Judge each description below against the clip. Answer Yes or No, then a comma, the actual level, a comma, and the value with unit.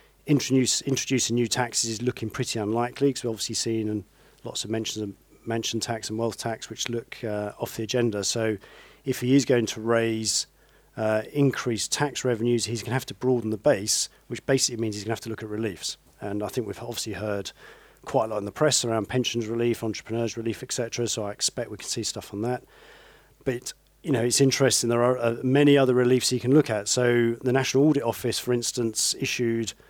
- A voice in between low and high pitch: No, low, 115 Hz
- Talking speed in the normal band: No, fast, 215 wpm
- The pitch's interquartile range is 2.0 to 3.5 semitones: Yes, narrow, 2.5 semitones